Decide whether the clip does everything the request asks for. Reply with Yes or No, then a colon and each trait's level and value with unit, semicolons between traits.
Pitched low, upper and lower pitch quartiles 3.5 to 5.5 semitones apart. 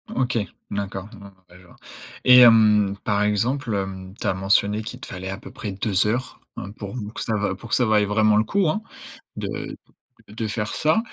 No: low, 105 Hz; average, 2.8 semitones